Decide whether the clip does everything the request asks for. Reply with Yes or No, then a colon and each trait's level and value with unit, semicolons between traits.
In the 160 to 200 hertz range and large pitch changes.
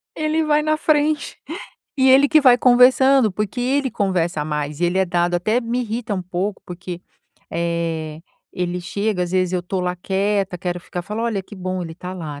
Yes: high, 190 Hz; wide, 5.8 semitones